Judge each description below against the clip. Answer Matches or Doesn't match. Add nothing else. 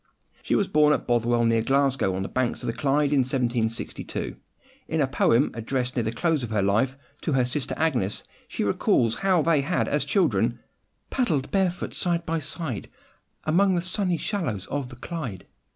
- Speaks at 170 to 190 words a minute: Matches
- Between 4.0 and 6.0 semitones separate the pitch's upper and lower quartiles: Matches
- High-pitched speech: Doesn't match